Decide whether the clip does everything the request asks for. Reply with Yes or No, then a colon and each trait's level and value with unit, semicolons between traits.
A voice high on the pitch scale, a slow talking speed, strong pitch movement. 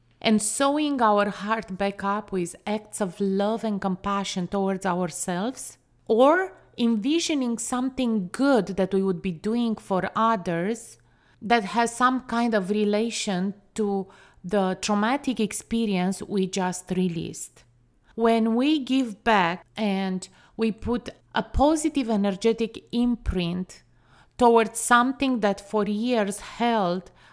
No: high, 210 Hz; slow, 120 wpm; average, 3.5 semitones